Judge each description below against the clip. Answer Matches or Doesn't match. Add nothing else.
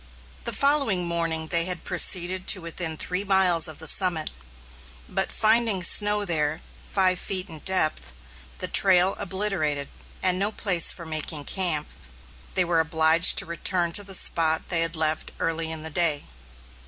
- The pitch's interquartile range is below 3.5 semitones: Matches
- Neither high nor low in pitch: Matches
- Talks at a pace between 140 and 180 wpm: Matches